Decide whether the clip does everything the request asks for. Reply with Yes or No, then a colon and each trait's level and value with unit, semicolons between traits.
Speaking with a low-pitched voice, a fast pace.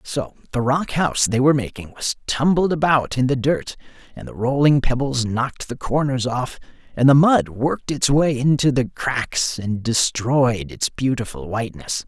No: low, 130 Hz; average, 175 wpm